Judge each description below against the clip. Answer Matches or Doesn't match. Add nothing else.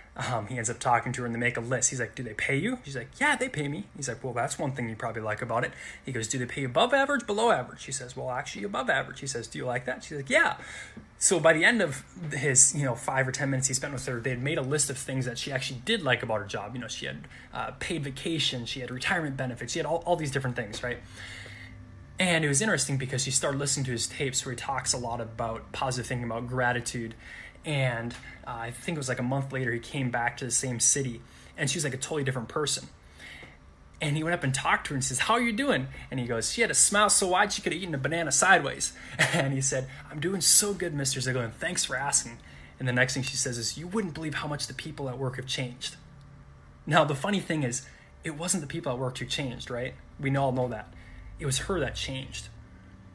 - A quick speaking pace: Matches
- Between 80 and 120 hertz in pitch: Doesn't match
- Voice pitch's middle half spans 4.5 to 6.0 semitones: Doesn't match